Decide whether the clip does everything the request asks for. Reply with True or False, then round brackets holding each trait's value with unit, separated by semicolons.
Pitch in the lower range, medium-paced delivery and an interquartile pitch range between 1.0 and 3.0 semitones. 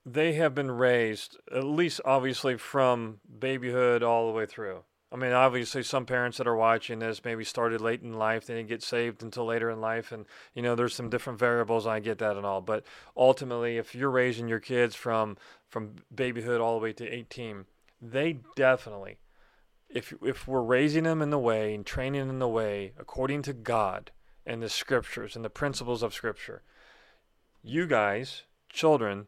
True (120 Hz; 190 wpm; 2.4 semitones)